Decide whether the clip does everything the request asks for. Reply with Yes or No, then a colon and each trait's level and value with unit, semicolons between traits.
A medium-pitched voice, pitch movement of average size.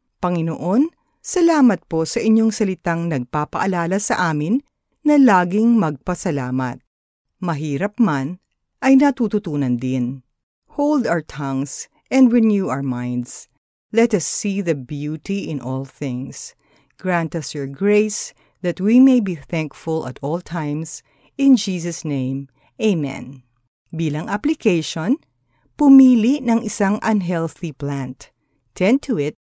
No: medium, 170 Hz; wide, 7.5 semitones